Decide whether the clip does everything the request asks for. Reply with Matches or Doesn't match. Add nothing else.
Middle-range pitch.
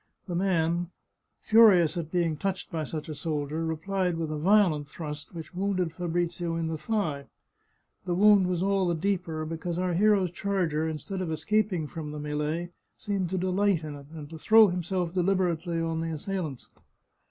Matches